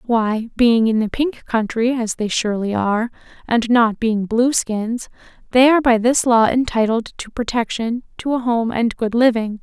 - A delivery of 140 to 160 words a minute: No, average, 175 wpm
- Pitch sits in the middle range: No, high, 230 Hz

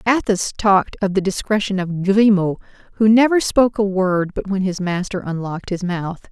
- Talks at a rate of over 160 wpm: Yes, average, 180 wpm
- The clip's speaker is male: No, female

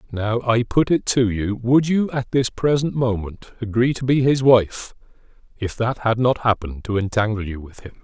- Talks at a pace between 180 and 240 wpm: Yes, average, 200 wpm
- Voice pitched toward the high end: No, low, 115 Hz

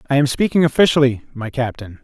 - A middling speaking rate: Yes, average, 175 wpm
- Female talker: No, male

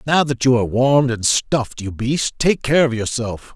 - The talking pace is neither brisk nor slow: No, fast, 220 wpm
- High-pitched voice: No, low, 125 Hz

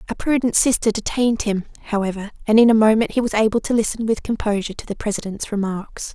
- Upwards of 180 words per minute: Yes, fast, 205 wpm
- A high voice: Yes, high, 215 Hz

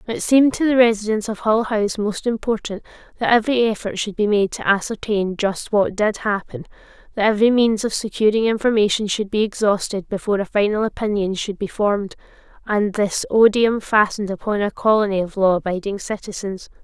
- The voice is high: Yes, high, 210 Hz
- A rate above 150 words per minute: Yes, average, 175 wpm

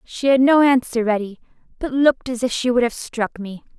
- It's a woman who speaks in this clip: Yes, female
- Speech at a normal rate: No, fast, 220 wpm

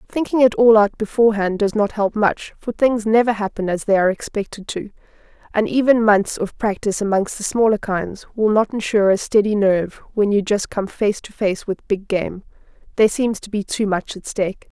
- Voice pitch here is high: Yes, high, 210 Hz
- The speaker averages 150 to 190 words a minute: No, fast, 205 wpm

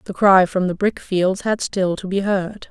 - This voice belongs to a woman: Yes, female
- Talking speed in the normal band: No, fast, 220 wpm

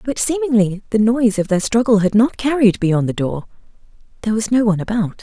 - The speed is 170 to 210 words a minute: Yes, fast, 205 wpm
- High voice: Yes, high, 220 Hz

